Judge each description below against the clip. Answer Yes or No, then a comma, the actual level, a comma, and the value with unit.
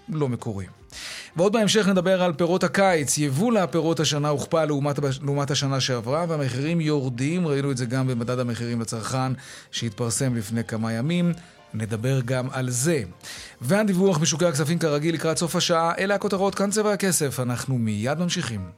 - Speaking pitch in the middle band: Yes, medium, 145 Hz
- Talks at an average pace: No, fast, 155 wpm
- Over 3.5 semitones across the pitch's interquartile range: Yes, wide, 5.5 semitones